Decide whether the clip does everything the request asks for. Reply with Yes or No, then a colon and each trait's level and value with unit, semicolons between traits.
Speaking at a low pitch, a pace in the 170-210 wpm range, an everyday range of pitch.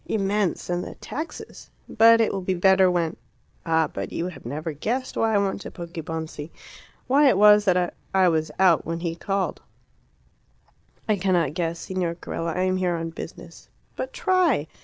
No: medium, 180 Hz; average, 175 wpm; average, 3.5 semitones